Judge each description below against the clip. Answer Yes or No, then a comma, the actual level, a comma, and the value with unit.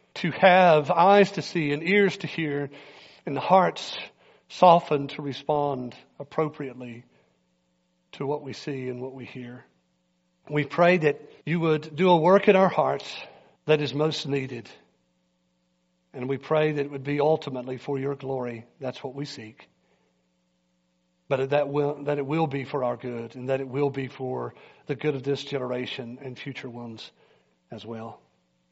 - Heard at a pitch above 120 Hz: Yes, low, 135 Hz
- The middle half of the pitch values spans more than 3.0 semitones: Yes, average, 4.1 semitones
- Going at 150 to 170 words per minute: Yes, average, 165 wpm